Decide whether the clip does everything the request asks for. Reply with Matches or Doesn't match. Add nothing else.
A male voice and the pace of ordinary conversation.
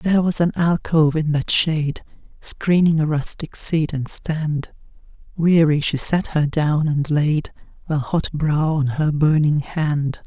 Doesn't match